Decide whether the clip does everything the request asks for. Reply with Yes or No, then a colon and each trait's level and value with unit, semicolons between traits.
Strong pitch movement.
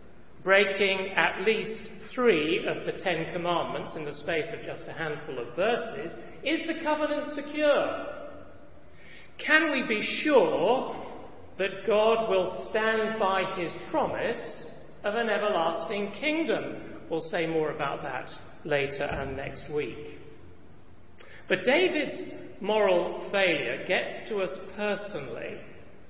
Yes: wide, 8.2 semitones